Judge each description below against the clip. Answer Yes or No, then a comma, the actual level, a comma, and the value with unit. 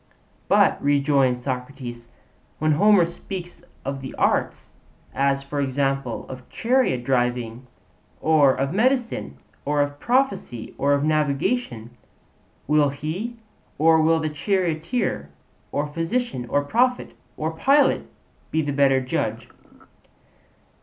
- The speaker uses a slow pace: Yes, slow, 115 wpm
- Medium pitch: Yes, medium, 145 Hz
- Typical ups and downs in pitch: Yes, average, 4.3 semitones